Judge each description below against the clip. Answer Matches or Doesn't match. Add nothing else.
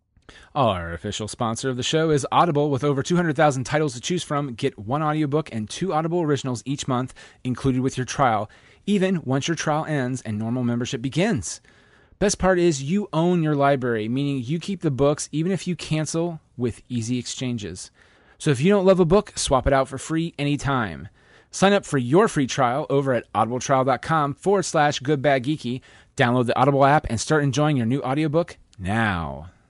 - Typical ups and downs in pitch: Matches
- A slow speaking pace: Doesn't match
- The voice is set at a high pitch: Doesn't match